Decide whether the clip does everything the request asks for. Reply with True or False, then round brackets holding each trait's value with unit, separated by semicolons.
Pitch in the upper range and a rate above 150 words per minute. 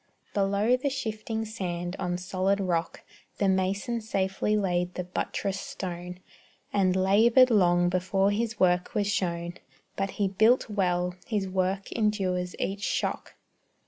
False (195 Hz; 135 wpm)